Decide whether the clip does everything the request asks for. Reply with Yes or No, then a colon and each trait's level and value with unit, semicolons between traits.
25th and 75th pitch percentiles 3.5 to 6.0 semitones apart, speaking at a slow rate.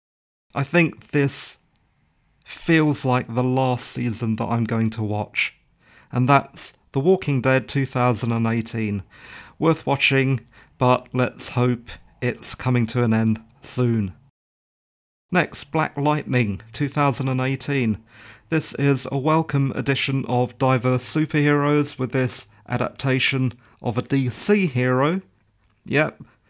No: average, 3.0 semitones; slow, 115 wpm